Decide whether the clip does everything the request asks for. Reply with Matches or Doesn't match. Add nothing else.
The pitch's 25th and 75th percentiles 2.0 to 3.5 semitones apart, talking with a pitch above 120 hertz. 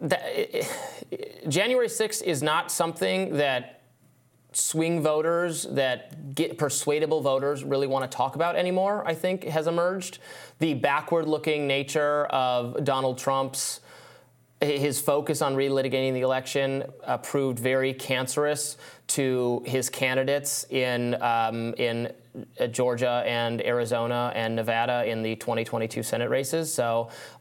Doesn't match